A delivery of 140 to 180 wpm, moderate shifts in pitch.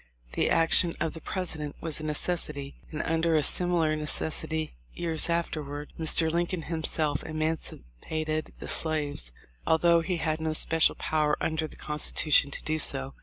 No: average, 155 wpm; narrow, 1.4 semitones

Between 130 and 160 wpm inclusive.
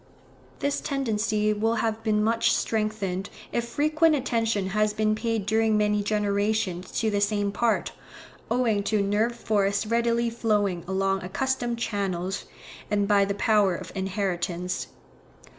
Yes: slow, 135 wpm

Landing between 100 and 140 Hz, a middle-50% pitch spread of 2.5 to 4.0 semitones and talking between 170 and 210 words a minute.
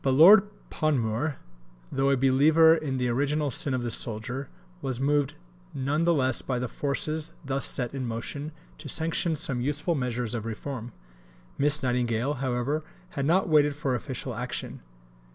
No: low, 135 Hz; average, 3.4 semitones; average, 160 wpm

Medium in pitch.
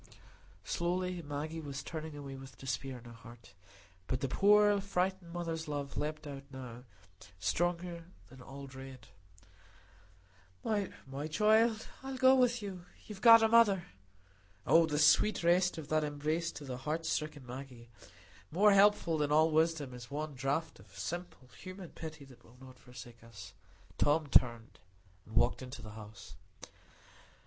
Yes: medium, 150 Hz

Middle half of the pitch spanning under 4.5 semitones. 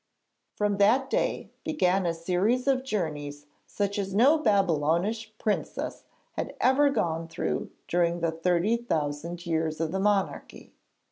No: average, 4.9 semitones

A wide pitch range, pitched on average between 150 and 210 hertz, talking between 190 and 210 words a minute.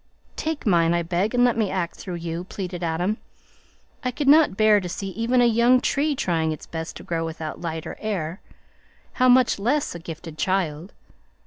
Yes: wide, 6.1 semitones; medium, 185 Hz; average, 195 wpm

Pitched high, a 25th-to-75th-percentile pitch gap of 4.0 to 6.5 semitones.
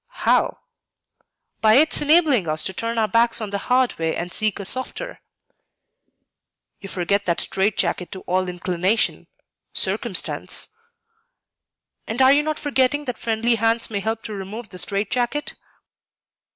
Yes: high, 220 Hz; average, 4.6 semitones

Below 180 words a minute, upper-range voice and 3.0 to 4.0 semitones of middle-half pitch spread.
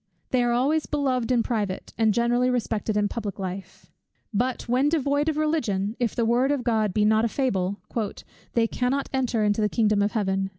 No: average, 195 wpm; high, 235 Hz; average, 3.6 semitones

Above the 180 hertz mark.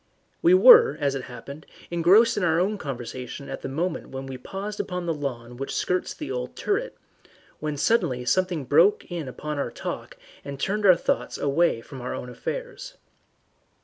No: medium, 160 Hz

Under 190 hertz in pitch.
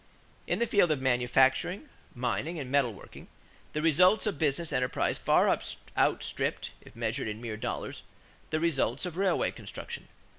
Yes: medium, 140 Hz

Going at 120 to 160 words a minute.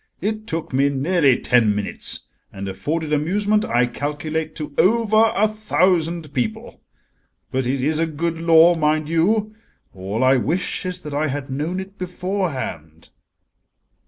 Yes: average, 145 wpm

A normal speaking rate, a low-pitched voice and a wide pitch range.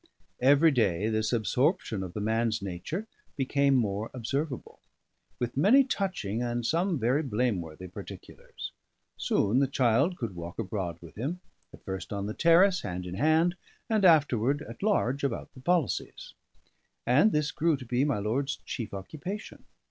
Yes: average, 155 wpm; low, 125 Hz; wide, 6.6 semitones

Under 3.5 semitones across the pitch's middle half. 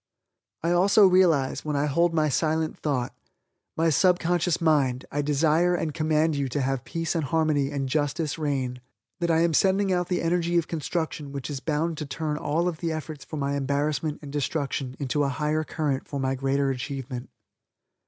Yes: average, 2.9 semitones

